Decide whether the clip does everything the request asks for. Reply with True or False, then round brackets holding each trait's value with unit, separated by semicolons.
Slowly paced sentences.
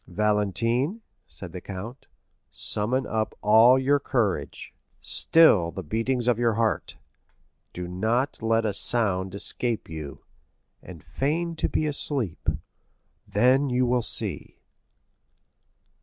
True (115 wpm)